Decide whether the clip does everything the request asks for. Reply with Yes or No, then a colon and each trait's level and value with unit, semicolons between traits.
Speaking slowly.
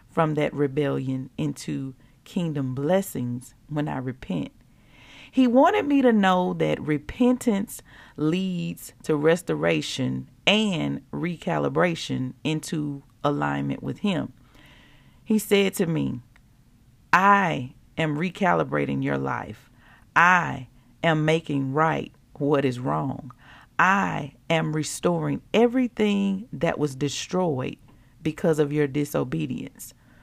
Yes: slow, 105 wpm